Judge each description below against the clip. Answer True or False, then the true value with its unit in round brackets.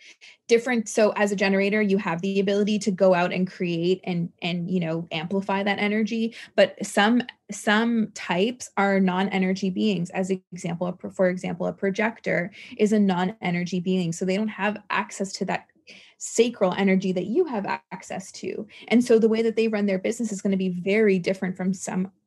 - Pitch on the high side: True (195 Hz)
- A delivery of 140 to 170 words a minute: False (190 wpm)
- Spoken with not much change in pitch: True (2.3 semitones)